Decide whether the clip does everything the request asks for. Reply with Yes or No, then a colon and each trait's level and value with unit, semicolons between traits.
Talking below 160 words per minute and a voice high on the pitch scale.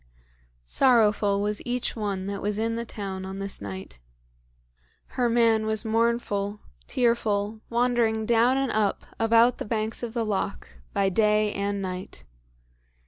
Yes: average, 140 wpm; high, 215 Hz